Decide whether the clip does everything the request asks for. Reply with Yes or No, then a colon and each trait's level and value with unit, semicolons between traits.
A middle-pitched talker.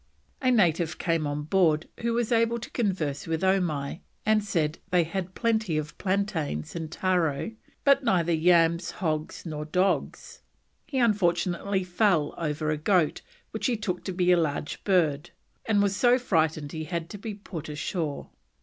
Yes: medium, 175 Hz